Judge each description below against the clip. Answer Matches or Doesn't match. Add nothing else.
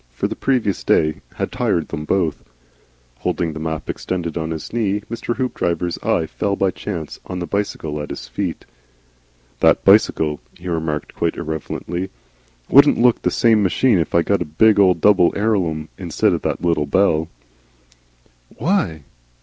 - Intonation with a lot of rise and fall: Doesn't match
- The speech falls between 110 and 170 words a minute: Matches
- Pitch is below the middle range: Matches